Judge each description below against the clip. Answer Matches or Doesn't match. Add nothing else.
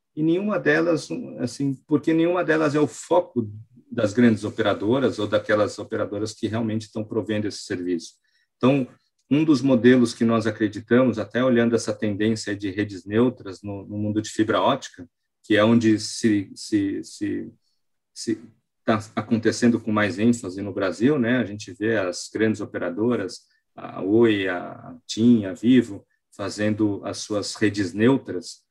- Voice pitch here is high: Doesn't match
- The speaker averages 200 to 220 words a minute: Doesn't match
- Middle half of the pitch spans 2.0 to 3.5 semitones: Matches